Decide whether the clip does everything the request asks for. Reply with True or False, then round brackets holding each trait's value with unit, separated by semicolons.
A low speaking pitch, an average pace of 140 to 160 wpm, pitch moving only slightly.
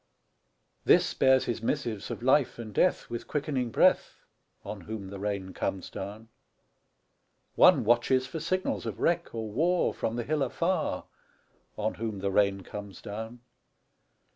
False (115 Hz; 145 wpm; 4.4 semitones)